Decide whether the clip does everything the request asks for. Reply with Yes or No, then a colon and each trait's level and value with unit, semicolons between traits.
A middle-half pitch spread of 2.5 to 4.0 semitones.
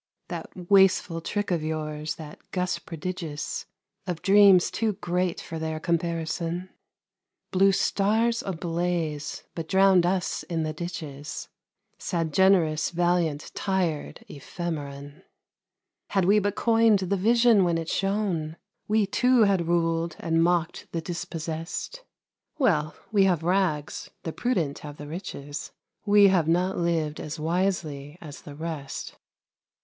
Yes: average, 3.4 semitones